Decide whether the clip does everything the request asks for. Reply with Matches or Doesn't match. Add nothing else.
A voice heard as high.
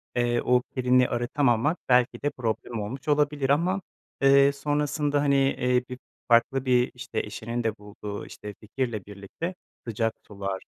Doesn't match